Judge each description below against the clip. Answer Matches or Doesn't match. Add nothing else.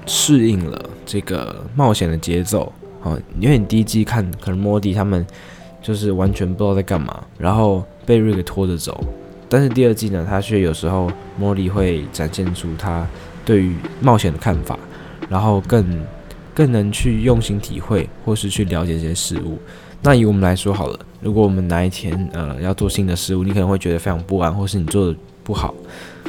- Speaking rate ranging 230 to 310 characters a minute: Matches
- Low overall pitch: Matches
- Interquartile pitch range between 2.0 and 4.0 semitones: Matches